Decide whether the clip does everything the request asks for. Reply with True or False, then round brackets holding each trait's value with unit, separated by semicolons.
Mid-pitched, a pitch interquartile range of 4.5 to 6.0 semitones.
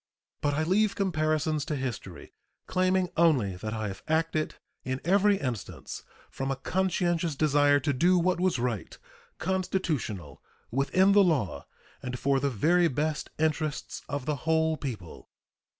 True (155 Hz; 5.1 semitones)